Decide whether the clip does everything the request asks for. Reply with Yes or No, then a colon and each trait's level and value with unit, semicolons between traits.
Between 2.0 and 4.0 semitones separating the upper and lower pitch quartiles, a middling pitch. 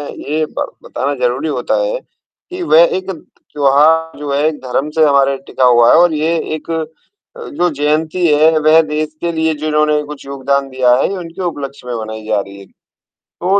Yes: average, 2.8 semitones; medium, 150 Hz